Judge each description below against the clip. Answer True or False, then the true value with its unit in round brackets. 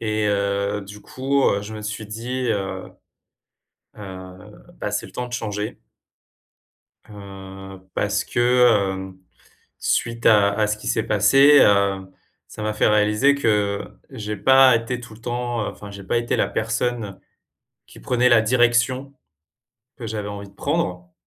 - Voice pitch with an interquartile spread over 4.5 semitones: False (3.2 semitones)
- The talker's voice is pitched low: True (105 Hz)